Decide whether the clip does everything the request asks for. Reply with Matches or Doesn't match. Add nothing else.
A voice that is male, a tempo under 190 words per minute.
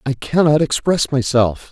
Matches